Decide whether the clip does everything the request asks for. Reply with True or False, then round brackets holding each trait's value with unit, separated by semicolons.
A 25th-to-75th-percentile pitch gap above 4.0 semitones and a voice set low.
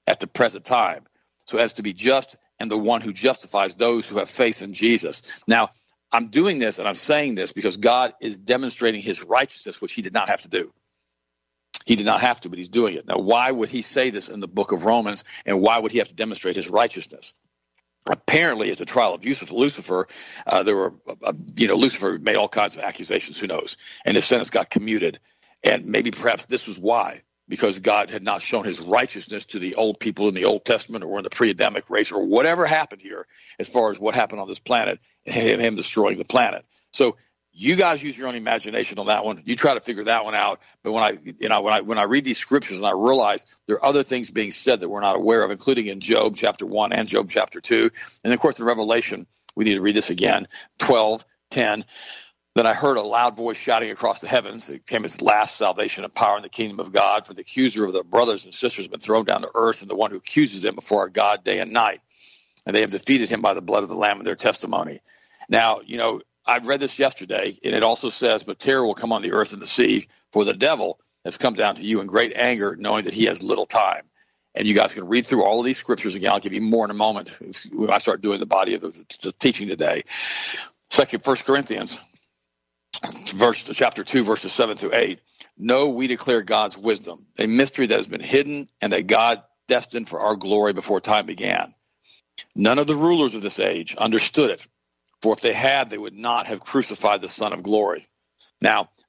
True (4.5 semitones; 115 Hz)